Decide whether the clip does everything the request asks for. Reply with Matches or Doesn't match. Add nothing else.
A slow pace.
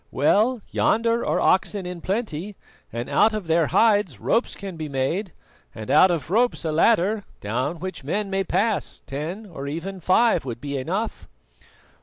Doesn't match